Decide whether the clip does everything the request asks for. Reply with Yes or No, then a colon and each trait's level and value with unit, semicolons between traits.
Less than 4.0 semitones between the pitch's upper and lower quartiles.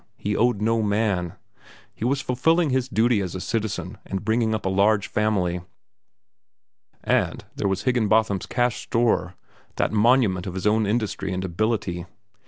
Yes: average, 3.4 semitones